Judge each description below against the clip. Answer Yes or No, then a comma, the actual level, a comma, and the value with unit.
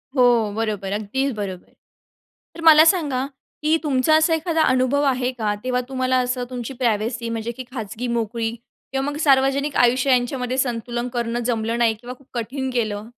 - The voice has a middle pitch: No, very high, 250 Hz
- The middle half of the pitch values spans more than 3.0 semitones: No, average, 2.7 semitones